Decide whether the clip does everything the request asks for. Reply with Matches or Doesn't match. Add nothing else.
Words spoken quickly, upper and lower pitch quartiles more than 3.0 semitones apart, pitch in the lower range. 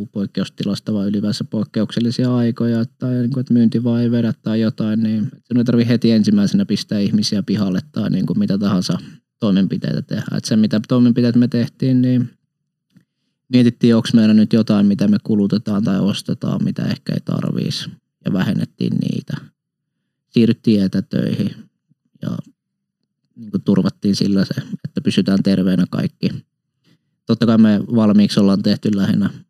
Doesn't match